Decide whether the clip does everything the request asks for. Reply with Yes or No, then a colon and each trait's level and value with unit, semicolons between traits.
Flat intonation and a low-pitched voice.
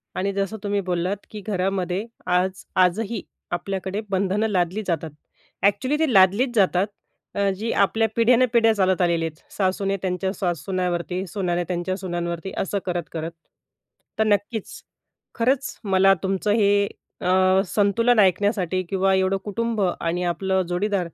No: narrow, 2.2 semitones; high, 190 Hz